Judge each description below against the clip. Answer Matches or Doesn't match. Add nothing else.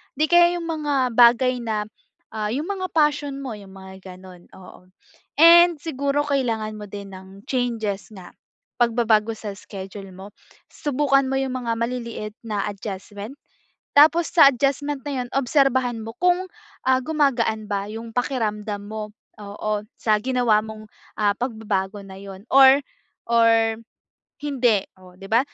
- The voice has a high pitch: Matches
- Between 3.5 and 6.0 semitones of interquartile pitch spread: Matches